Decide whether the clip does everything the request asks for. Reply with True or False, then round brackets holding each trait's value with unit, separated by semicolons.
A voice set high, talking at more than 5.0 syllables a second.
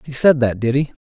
False (130 Hz; 5.9 syllables/s)